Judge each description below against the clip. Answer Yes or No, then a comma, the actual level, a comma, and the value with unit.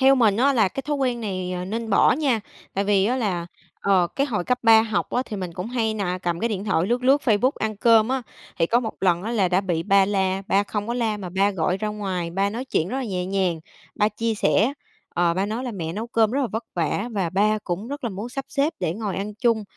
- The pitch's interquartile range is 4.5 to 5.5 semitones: No, average, 3.8 semitones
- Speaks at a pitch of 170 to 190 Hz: No, high, 210 Hz